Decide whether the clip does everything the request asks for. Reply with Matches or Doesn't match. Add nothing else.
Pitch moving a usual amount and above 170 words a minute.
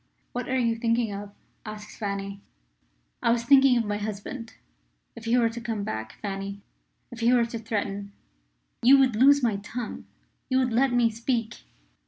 Matches